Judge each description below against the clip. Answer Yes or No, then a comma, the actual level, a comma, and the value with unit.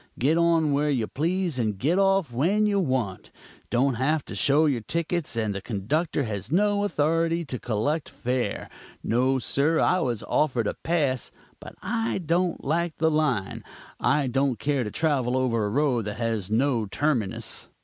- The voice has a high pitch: No, medium, 140 Hz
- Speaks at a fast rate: No, average, 170 wpm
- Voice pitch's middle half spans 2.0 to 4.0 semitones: No, wide, 5.6 semitones